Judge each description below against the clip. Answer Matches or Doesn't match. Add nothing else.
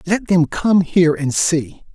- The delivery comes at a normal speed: Matches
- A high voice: Doesn't match